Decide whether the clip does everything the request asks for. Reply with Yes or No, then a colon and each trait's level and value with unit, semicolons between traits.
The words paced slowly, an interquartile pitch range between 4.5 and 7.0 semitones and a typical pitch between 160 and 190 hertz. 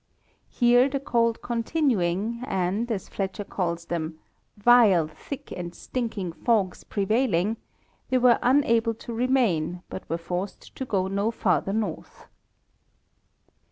No: slow, 125 wpm; average, 4.9 semitones; high, 215 Hz